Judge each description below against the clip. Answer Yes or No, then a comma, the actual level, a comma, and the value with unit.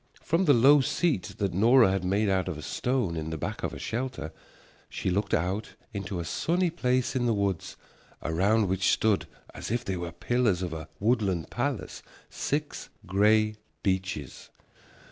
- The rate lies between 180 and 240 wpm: No, average, 170 wpm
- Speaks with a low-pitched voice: Yes, low, 100 Hz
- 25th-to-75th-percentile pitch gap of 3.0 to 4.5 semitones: No, average, 5.1 semitones